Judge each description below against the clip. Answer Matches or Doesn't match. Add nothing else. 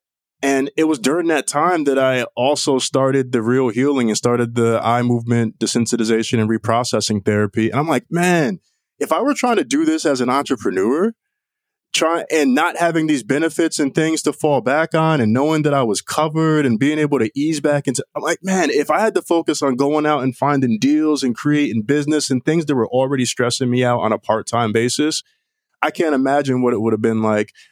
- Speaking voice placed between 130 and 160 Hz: Matches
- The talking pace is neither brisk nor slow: Doesn't match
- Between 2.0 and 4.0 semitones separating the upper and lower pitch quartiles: Doesn't match